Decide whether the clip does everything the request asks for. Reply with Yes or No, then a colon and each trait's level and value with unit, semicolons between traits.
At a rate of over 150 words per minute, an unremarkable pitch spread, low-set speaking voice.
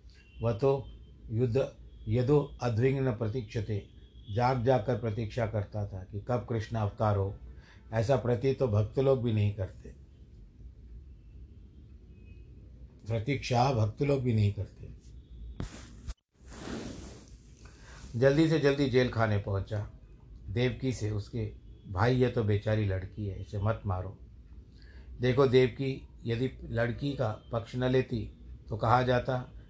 No: average, 125 wpm; average, 4.2 semitones; low, 115 Hz